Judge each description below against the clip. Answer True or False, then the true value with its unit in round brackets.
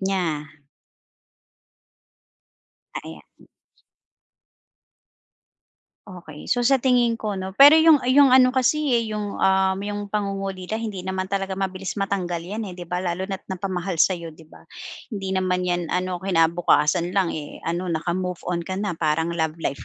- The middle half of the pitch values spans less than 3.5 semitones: True (2.7 semitones)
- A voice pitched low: False (190 Hz)